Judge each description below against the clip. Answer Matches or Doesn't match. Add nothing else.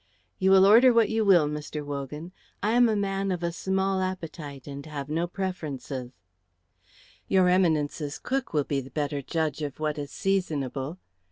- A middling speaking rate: Matches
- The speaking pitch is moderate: Matches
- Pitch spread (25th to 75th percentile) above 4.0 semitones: Matches